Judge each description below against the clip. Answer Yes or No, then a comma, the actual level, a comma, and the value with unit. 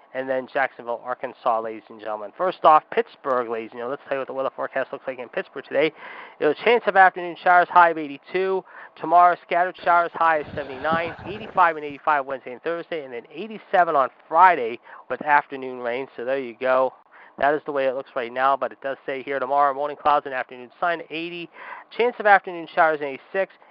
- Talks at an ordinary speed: No, fast, 210 wpm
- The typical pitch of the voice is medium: Yes, medium, 150 Hz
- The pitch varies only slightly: No, average, 5.0 semitones